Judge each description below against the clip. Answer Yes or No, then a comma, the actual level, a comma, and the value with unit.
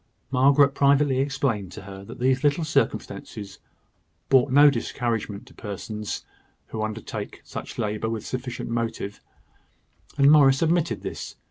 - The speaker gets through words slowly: Yes, slow, 130 wpm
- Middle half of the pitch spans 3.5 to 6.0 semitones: Yes, average, 4.6 semitones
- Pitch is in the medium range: No, low, 125 Hz